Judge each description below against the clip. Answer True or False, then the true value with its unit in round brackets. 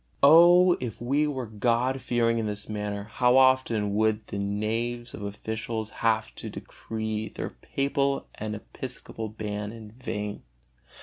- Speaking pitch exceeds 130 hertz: False (110 Hz)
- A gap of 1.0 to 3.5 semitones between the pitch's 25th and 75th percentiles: True (3.1 semitones)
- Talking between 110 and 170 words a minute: True (140 wpm)